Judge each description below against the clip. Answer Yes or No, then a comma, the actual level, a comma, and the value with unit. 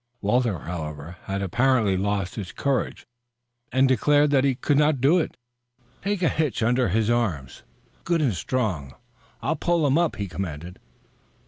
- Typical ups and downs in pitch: No, wide, 7.2 semitones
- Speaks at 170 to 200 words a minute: No, average, 155 wpm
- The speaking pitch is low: Yes, low, 120 Hz